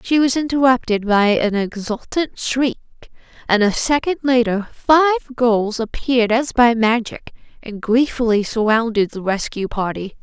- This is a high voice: Yes, high, 235 Hz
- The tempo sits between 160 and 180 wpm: No, slow, 135 wpm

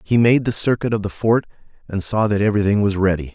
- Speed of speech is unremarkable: No, fast, 235 wpm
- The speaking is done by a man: Yes, male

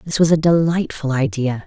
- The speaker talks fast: No, average, 180 wpm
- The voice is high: No, medium, 150 Hz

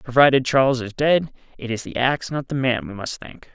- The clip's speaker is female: No, male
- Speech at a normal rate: No, fast, 235 wpm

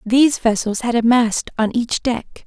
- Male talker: No, female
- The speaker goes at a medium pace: Yes, average, 195 wpm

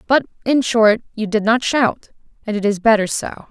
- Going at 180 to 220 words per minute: Yes, fast, 205 wpm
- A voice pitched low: No, high, 225 Hz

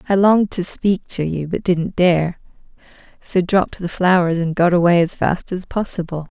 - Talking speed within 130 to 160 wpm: No, average, 190 wpm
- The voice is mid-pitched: Yes, medium, 180 Hz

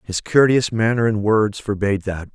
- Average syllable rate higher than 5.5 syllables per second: No, 5.0 syllables/s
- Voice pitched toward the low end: Yes, low, 105 Hz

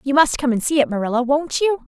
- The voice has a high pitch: Yes, very high, 275 Hz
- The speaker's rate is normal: No, fast, 245 wpm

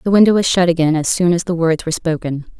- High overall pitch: No, medium, 170 Hz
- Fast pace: Yes, fast, 280 wpm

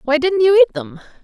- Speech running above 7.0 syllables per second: No, 5.9 syllables/s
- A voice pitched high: Yes, very high, 305 Hz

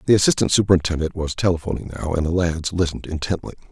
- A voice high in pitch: No, very low, 85 Hz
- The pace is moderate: Yes, average, 180 wpm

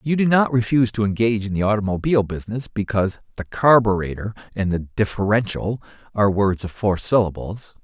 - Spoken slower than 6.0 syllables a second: No, 6.1 syllables/s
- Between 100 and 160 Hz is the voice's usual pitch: Yes, low, 105 Hz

